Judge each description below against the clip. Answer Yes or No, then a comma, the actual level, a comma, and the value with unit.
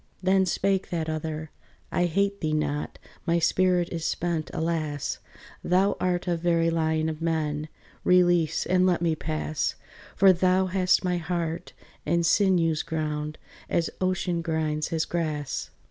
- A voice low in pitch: No, medium, 165 Hz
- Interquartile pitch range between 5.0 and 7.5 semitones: No, narrow, 2.4 semitones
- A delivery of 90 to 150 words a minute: Yes, average, 145 wpm